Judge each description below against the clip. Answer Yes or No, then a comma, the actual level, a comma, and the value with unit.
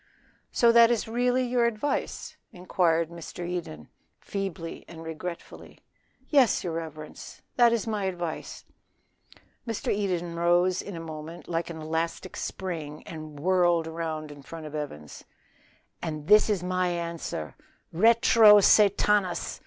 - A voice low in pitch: No, medium, 175 Hz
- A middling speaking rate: No, slow, 130 wpm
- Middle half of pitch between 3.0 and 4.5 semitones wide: Yes, average, 4.1 semitones